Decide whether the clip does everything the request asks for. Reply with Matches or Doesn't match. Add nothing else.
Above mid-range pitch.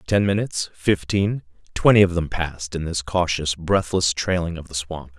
Doesn't match